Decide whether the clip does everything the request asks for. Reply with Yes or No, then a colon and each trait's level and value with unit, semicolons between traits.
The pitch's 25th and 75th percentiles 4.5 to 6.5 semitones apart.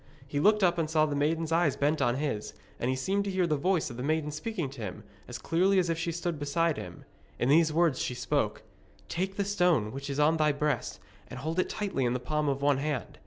No: average, 3.7 semitones